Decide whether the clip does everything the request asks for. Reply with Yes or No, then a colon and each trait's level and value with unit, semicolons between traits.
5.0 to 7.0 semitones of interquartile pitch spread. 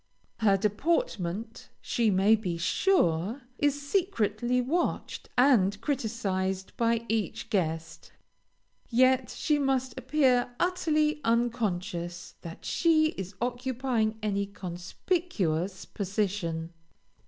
Yes: wide, 5.5 semitones